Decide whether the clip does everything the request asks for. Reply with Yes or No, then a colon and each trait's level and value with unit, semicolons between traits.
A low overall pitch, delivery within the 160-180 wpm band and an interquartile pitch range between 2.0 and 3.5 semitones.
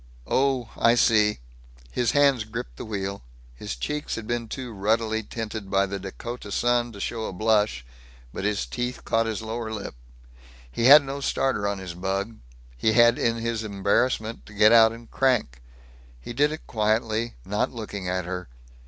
Yes: low, 110 Hz; average, 175 wpm; average, 2.8 semitones